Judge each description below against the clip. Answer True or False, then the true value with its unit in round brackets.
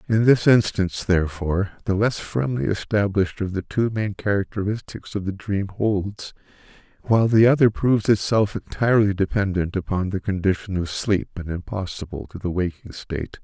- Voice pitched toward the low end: True (100 Hz)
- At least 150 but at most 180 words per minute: True (155 wpm)